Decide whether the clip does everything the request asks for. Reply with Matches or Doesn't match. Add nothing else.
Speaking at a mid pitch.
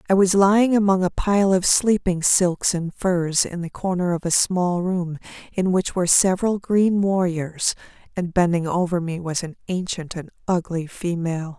Matches